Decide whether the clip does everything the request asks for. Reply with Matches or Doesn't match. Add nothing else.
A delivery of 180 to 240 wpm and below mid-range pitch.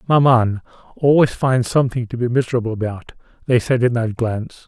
Doesn't match